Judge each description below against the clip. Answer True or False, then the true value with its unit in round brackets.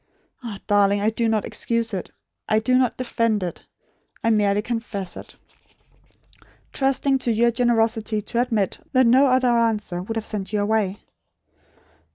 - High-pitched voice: True (225 Hz)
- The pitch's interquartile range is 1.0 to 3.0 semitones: True (2.4 semitones)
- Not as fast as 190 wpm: True (155 wpm)